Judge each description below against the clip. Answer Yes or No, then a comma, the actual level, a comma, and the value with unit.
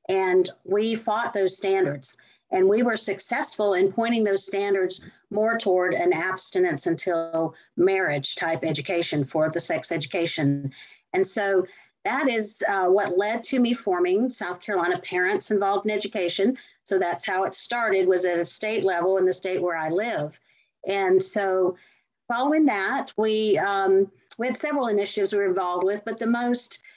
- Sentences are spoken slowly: No, average, 165 wpm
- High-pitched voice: Yes, high, 195 Hz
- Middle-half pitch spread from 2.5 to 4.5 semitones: Yes, average, 3.4 semitones